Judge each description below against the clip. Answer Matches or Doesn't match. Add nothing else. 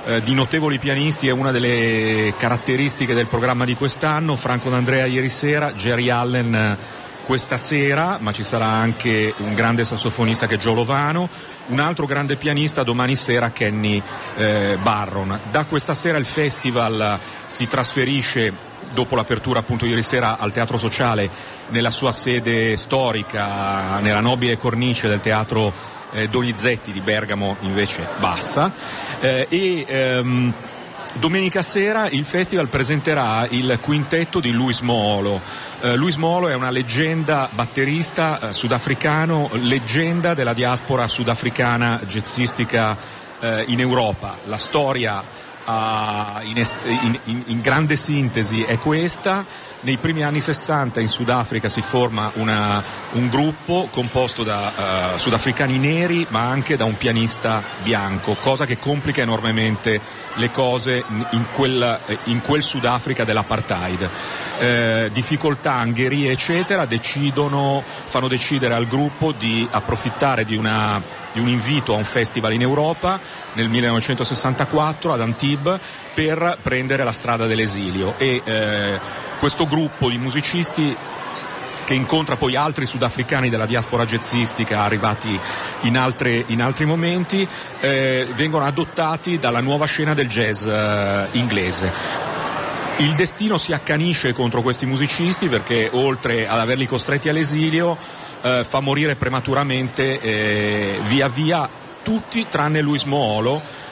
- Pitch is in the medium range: Doesn't match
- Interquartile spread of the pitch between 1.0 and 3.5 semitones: Doesn't match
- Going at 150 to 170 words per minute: Doesn't match